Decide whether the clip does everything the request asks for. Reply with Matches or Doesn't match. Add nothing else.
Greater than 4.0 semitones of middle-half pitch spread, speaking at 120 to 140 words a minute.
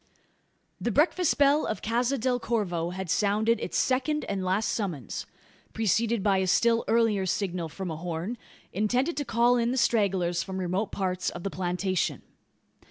Doesn't match